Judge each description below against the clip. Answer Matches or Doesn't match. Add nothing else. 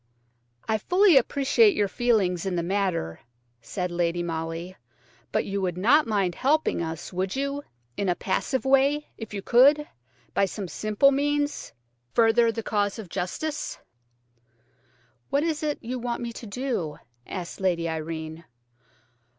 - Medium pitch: Doesn't match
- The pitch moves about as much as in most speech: Doesn't match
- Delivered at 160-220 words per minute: Doesn't match